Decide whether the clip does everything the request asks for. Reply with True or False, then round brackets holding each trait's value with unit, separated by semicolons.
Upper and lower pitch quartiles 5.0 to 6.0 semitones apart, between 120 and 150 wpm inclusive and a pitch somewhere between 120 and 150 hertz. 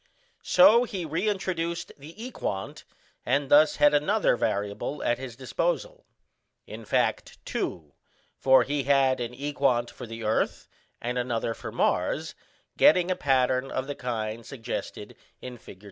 True (5.6 semitones; 140 wpm; 135 Hz)